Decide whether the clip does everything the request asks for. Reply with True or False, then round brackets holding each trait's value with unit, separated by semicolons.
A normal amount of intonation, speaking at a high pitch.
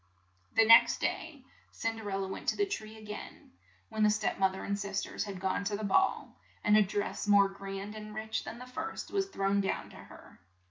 False (2.2 semitones; 210 Hz)